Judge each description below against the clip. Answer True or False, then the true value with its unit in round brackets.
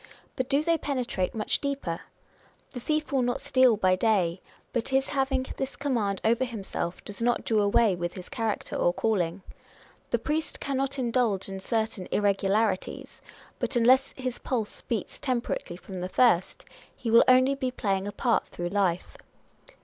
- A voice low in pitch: False (230 Hz)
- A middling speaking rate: True (160 wpm)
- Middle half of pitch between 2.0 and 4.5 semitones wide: False (4.9 semitones)